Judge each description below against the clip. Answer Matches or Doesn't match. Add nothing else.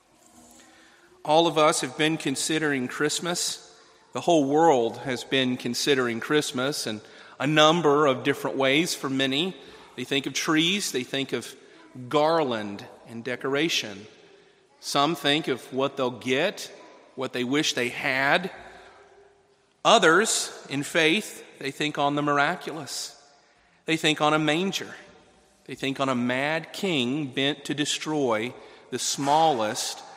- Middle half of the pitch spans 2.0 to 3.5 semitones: Matches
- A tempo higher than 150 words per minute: Doesn't match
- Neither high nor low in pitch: Matches